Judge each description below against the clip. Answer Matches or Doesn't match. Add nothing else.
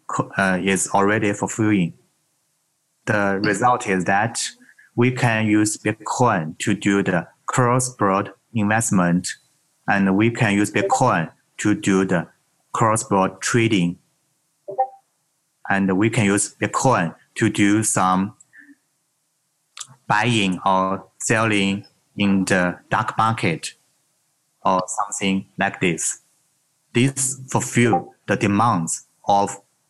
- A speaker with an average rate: Doesn't match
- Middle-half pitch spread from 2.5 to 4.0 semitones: Doesn't match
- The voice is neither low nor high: Doesn't match